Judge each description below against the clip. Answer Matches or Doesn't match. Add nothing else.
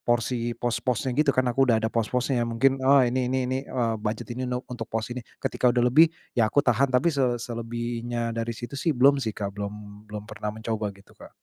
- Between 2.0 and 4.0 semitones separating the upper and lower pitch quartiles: Matches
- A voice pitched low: Matches